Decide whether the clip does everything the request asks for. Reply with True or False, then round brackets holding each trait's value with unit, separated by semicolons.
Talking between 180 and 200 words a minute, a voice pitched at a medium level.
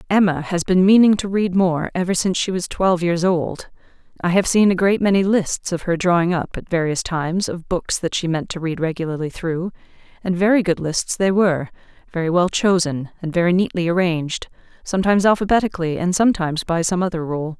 True (190 wpm; 180 Hz)